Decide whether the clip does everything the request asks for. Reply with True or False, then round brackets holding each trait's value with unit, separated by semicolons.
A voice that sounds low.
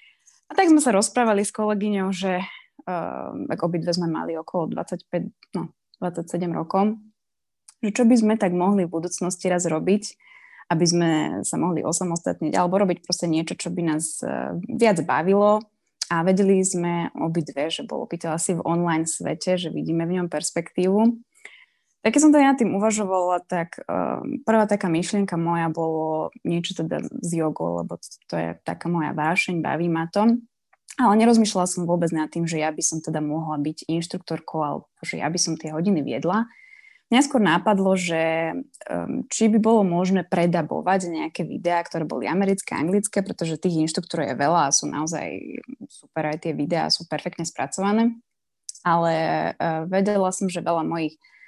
False (175 Hz)